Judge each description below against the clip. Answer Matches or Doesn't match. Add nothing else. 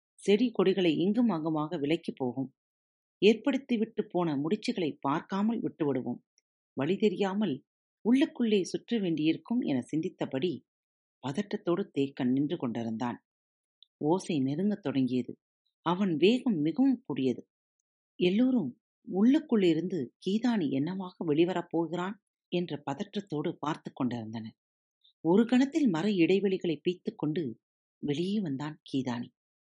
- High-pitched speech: Doesn't match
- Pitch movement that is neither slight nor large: Doesn't match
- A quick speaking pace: Doesn't match